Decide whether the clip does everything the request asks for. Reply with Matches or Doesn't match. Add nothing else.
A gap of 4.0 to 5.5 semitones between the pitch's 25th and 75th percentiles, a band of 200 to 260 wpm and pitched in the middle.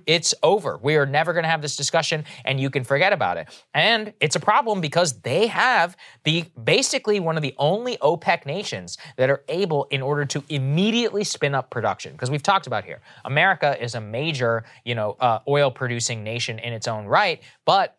Matches